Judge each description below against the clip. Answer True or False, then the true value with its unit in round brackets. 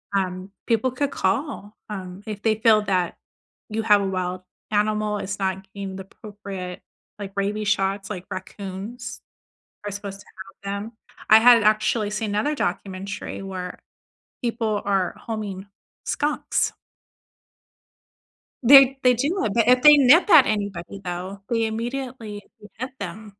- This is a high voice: True (210 Hz)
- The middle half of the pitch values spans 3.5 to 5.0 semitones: False (2.8 semitones)